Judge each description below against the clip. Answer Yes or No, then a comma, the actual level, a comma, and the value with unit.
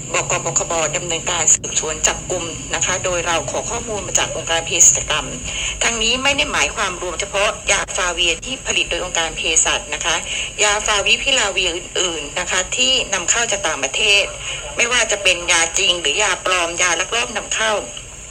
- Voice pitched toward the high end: No, medium, 180 Hz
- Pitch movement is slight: No, average, 3.6 semitones